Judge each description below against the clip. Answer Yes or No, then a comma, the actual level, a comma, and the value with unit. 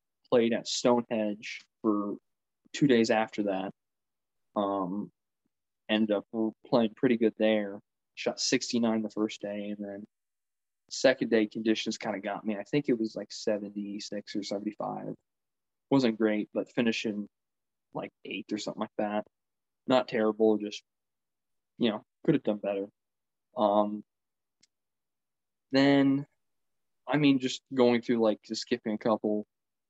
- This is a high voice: No, low, 110 Hz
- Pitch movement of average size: No, narrow, 2.1 semitones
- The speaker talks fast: No, slow, 135 wpm